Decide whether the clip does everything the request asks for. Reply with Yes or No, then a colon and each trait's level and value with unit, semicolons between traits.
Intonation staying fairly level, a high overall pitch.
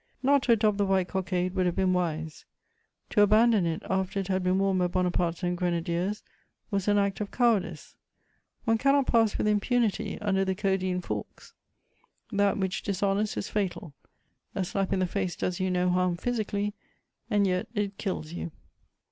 Yes: narrow, 2.3 semitones; high, 195 Hz